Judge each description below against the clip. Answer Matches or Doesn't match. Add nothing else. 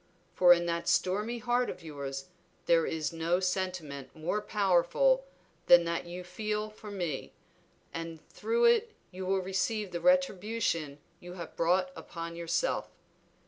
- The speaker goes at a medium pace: Matches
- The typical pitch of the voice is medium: Matches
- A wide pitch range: Doesn't match